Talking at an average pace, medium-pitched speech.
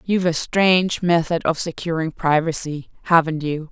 Yes: average, 145 wpm; medium, 165 Hz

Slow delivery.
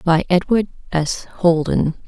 Yes: slow, 115 wpm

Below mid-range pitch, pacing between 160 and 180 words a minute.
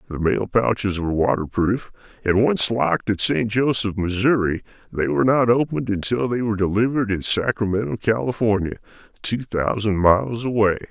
No: low, 110 Hz; average, 150 wpm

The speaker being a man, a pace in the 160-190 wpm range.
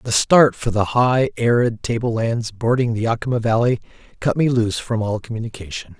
Yes: male; average, 180 wpm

